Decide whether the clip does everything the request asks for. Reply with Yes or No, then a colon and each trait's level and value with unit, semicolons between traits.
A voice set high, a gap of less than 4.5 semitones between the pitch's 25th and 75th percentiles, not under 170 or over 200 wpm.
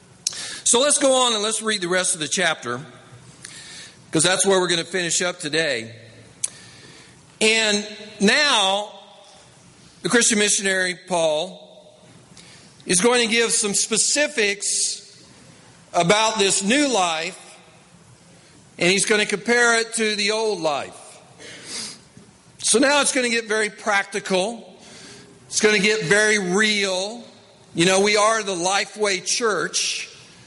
No: high, 200 Hz; average, 3.6 semitones; slow, 135 wpm